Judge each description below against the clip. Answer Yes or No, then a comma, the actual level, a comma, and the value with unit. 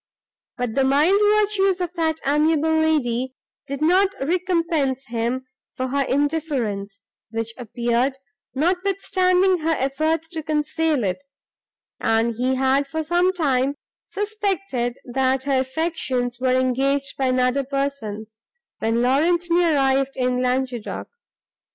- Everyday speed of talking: No, slow, 120 wpm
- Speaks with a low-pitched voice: No, very high, 275 Hz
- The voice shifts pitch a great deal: No, average, 4.3 semitones